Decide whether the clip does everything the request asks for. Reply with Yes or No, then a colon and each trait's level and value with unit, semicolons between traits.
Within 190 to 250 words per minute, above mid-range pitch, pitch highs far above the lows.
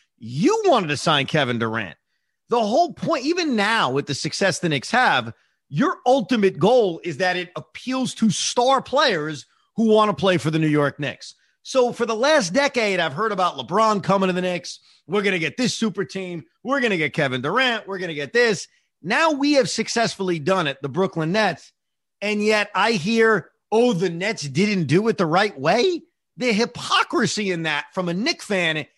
Yes: average, 200 wpm; high, 195 Hz; wide, 6.4 semitones